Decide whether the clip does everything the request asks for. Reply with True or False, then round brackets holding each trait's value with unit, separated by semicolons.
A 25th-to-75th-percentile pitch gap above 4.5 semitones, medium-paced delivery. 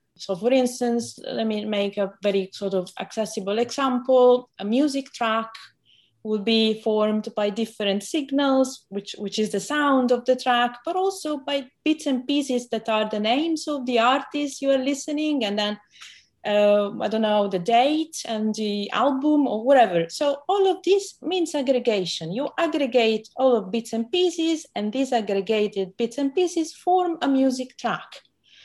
True (5.0 semitones; 170 wpm)